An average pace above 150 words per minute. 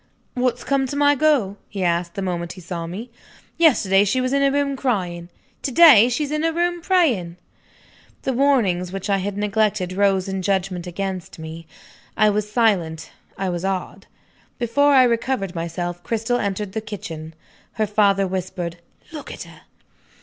Yes: average, 170 wpm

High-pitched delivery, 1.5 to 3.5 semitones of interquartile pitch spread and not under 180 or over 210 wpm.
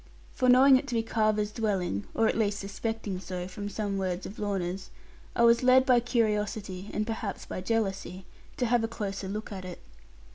Yes: high, 210 Hz; average, 2.9 semitones; average, 190 wpm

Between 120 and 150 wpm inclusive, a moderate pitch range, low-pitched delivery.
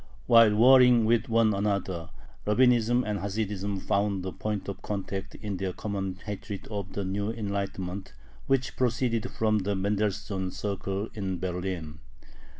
No: average, 140 wpm; narrow, 2.2 semitones; low, 100 Hz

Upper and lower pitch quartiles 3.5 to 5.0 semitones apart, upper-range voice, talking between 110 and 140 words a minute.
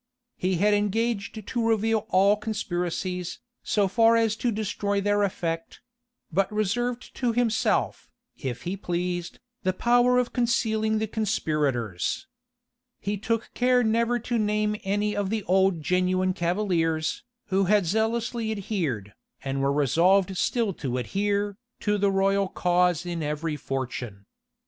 Yes: average, 3.8 semitones; high, 200 Hz; slow, 135 wpm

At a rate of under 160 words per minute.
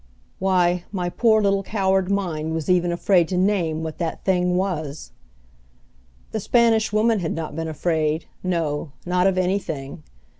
Yes: average, 150 wpm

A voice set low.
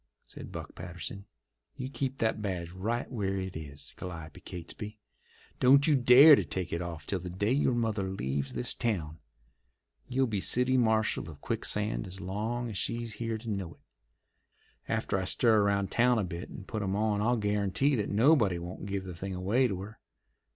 Yes: low, 100 Hz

